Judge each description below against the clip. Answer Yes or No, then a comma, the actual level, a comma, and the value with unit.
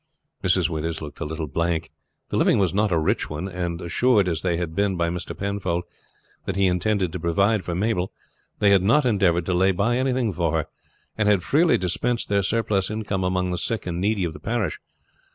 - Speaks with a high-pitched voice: No, very low, 95 Hz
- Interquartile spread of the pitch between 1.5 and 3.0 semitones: No, average, 3.4 semitones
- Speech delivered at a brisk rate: Yes, fast, 210 wpm